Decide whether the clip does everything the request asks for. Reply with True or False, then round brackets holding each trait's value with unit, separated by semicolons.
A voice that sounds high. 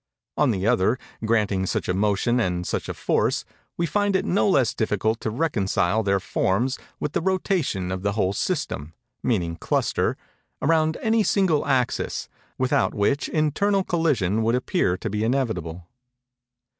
False (115 Hz)